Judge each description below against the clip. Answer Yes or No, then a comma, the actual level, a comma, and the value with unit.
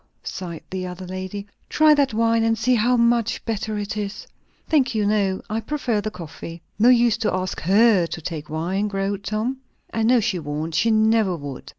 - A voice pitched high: Yes, high, 210 Hz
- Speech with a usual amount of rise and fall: Yes, average, 3.8 semitones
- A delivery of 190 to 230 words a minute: Yes, average, 195 wpm